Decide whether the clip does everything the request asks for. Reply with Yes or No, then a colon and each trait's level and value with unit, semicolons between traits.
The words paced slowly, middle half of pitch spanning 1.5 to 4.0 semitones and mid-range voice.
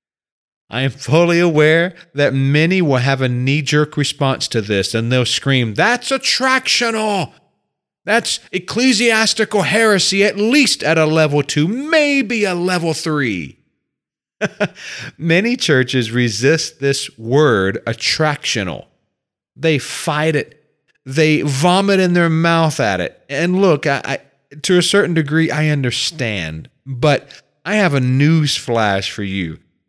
No: slow, 130 wpm; average, 5.3 semitones; medium, 155 Hz